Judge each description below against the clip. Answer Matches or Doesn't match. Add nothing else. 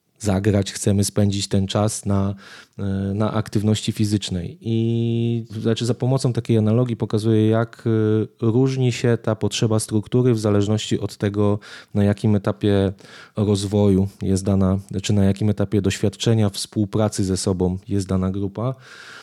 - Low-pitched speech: Matches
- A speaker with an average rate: Matches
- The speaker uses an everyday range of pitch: Doesn't match